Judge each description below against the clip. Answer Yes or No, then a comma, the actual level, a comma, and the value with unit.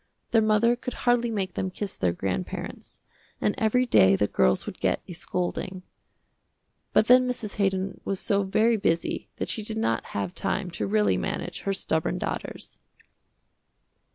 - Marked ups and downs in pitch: Yes, wide, 5.7 semitones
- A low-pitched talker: No, high, 195 Hz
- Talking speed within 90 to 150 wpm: No, average, 160 wpm